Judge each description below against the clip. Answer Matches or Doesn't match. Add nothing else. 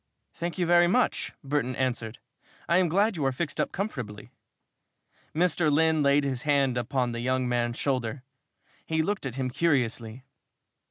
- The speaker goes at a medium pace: Matches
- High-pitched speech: Doesn't match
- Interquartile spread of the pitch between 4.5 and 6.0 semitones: Matches